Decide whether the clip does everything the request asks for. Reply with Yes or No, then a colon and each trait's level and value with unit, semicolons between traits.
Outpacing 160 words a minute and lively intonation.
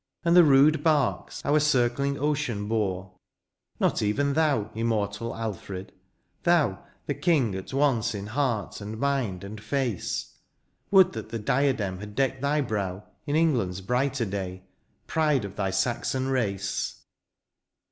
No: average, 140 wpm; wide, 5.7 semitones